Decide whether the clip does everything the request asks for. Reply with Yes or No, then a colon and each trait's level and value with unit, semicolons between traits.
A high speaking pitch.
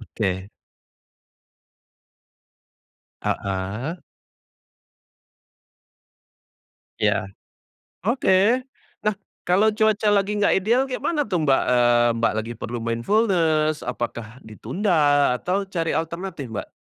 No: medium, 165 Hz